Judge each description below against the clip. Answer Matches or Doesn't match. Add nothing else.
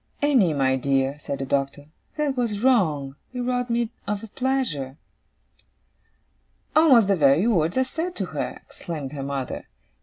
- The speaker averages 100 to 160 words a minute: Matches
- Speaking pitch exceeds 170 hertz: Matches